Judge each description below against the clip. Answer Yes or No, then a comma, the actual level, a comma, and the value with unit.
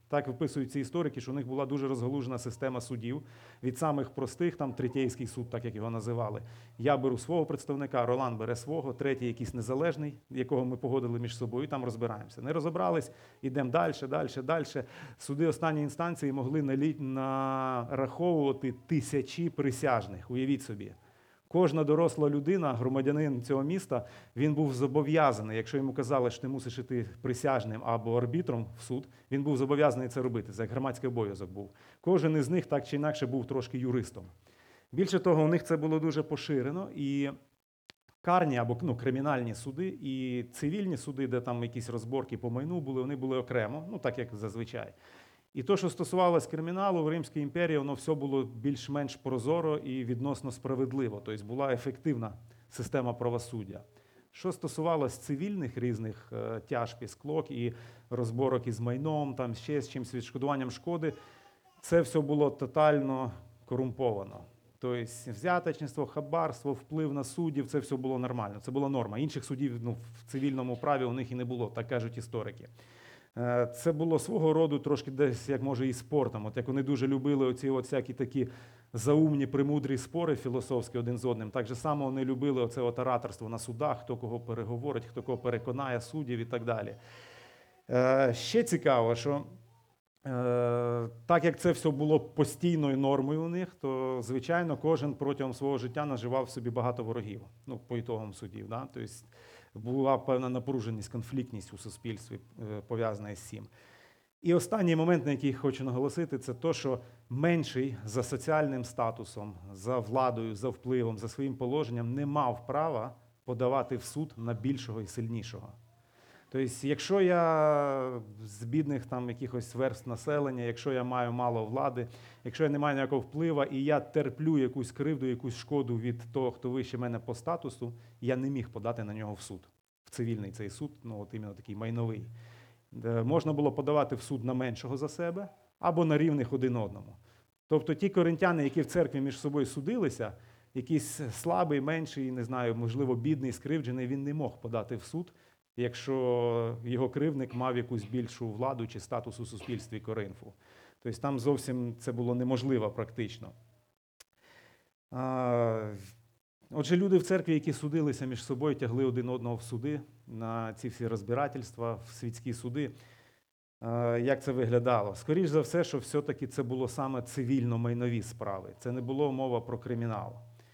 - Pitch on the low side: Yes, low, 130 Hz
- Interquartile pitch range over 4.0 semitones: No, average, 3.3 semitones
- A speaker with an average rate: No, fast, 160 wpm